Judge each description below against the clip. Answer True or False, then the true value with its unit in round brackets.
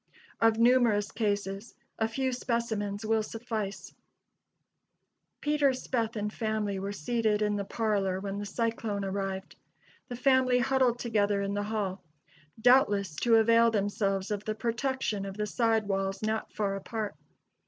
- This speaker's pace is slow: False (145 wpm)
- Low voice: False (215 Hz)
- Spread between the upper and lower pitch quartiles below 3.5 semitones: True (2.6 semitones)